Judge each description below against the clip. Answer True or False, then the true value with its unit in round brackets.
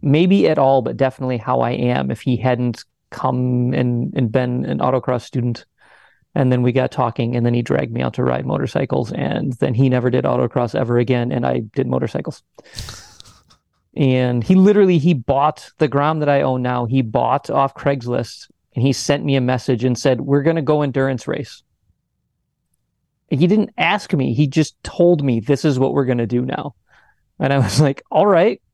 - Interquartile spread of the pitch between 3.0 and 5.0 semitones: False (2.4 semitones)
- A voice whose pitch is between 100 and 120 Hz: False (130 Hz)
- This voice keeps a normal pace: True (195 wpm)